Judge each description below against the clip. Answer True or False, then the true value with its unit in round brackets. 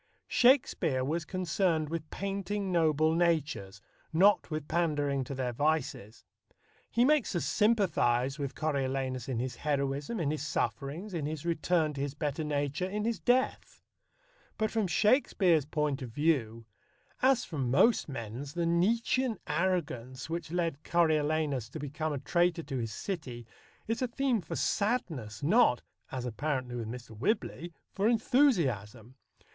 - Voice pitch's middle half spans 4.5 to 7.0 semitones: True (5.6 semitones)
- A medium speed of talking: True (145 wpm)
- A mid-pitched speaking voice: True (155 Hz)